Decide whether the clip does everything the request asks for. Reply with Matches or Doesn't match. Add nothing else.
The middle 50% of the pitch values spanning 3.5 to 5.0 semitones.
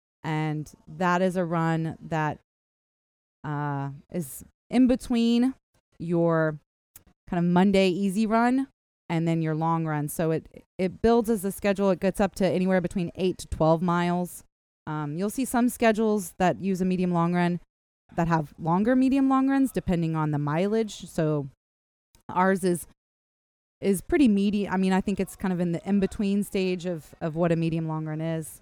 Matches